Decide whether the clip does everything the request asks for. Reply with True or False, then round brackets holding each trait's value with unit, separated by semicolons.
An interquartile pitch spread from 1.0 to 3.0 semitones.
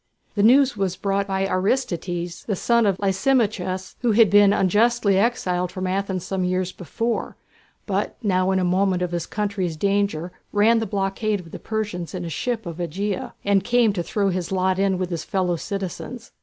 True (2.4 semitones)